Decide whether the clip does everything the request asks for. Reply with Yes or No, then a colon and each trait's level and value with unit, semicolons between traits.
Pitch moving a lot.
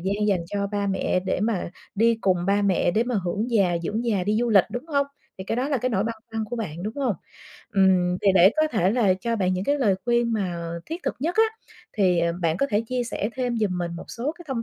No: average, 4.2 semitones